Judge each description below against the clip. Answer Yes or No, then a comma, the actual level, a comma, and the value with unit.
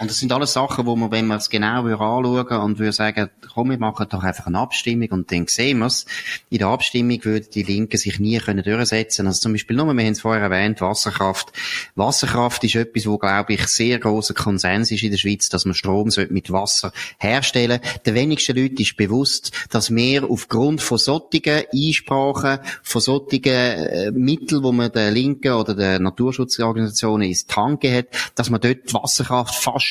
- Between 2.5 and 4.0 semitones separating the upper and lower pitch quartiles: Yes, average, 3.2 semitones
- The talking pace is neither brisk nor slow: No, fast, 200 wpm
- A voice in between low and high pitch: No, low, 115 Hz